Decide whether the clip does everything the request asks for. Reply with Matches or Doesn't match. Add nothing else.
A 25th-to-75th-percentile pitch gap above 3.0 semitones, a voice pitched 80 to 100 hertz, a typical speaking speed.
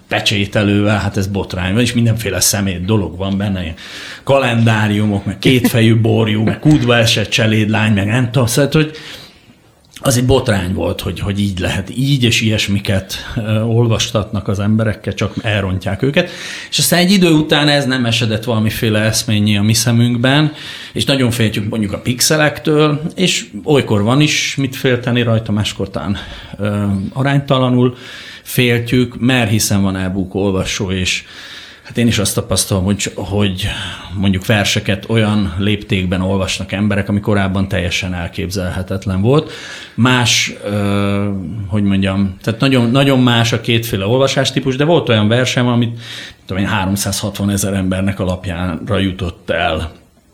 Doesn't match